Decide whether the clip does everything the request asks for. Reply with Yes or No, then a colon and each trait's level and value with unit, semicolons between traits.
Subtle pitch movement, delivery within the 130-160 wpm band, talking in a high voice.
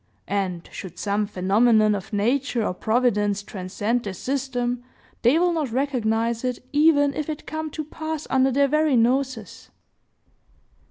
No: average, 5.0 semitones; average, 145 wpm; high, 245 Hz